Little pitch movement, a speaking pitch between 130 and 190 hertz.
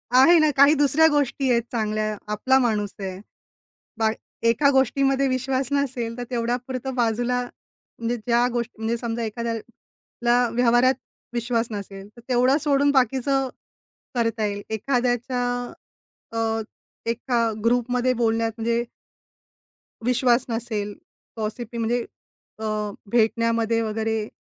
No: narrow, 2.2 semitones; high, 240 Hz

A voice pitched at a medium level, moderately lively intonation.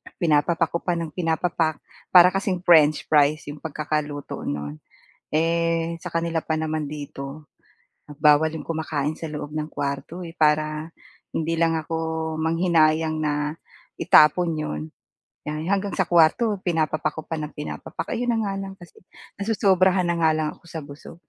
No: medium, 160 Hz; narrow, 2.1 semitones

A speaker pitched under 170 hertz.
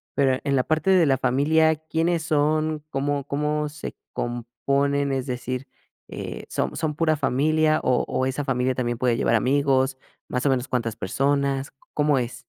Yes: medium, 140 Hz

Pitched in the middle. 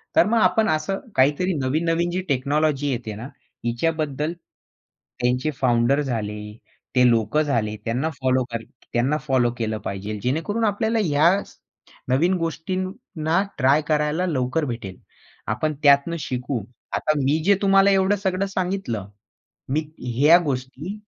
Yes: medium, 150 Hz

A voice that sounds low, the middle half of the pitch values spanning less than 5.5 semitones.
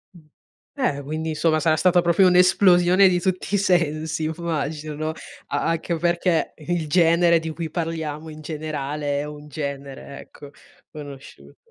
No: medium, 160 Hz; narrow, 2.6 semitones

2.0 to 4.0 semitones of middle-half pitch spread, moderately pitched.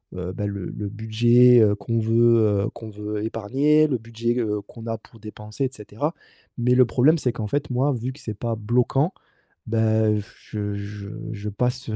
No: average, 2.8 semitones; low, 115 Hz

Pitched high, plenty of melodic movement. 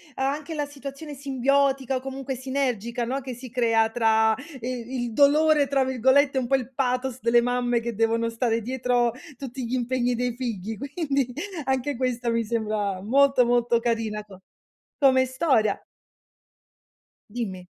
No: very high, 250 Hz; average, 2.7 semitones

